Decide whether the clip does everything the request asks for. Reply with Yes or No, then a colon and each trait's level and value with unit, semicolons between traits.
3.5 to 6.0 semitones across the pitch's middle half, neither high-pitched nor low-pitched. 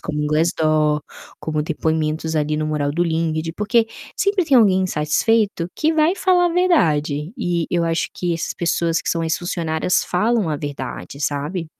Yes: average, 4.4 semitones; medium, 165 Hz